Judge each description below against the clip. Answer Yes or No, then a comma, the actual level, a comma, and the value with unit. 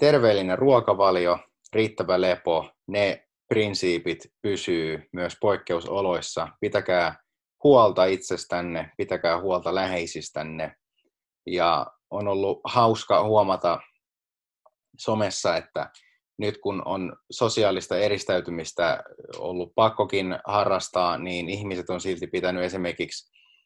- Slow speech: Yes, slow, 90 wpm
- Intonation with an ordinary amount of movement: No, narrow, 2.2 semitones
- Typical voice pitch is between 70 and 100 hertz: Yes, very low, 90 Hz